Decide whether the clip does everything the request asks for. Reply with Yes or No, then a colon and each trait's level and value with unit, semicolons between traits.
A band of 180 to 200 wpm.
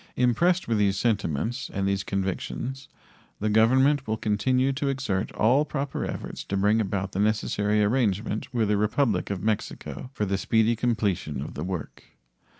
No: average, 160 wpm